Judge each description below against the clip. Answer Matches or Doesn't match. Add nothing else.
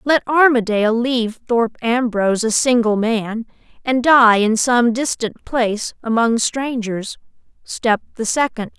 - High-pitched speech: Matches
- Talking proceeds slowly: Matches